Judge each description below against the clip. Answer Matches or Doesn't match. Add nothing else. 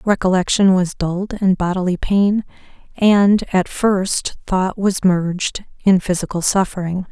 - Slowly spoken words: Matches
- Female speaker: Matches